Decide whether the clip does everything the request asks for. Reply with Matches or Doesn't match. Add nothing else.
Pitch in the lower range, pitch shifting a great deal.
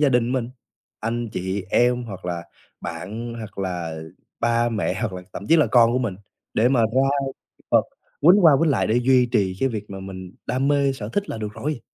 Doesn't match